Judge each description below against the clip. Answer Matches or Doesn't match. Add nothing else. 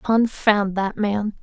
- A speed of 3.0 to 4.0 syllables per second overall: Matches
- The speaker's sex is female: Matches